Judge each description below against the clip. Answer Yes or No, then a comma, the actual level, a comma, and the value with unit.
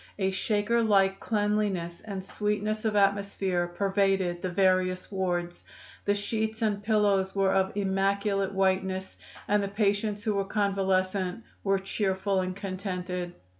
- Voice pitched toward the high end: Yes, high, 195 Hz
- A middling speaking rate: No, slow, 130 wpm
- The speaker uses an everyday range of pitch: No, narrow, 1.5 semitones